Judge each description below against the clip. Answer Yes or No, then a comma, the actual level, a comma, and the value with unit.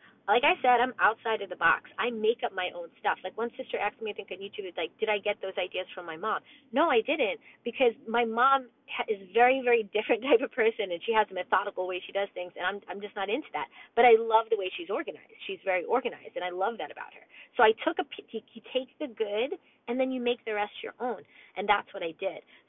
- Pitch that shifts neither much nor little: Yes, average, 5.0 semitones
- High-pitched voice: Yes, high, 225 Hz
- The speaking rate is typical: No, fast, 265 wpm